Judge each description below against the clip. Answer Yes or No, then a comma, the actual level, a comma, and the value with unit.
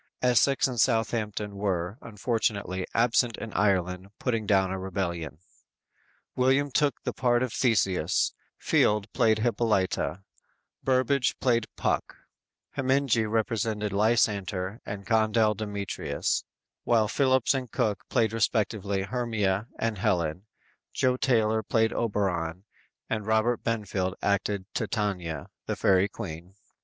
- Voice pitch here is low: Yes, low, 110 Hz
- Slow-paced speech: Yes, slow, 115 wpm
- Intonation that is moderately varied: Yes, average, 3.3 semitones